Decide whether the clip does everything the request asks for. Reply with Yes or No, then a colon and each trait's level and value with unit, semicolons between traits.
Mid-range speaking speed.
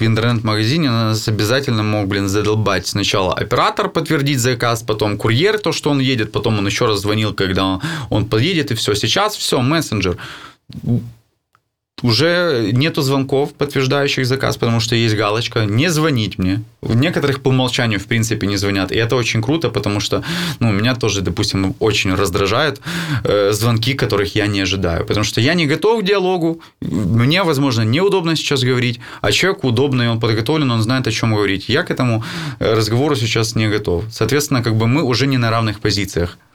No: fast, 170 wpm